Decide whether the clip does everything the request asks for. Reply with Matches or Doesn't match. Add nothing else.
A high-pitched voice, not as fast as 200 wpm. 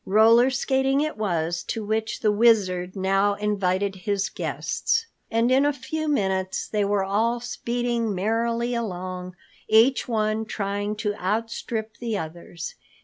Matches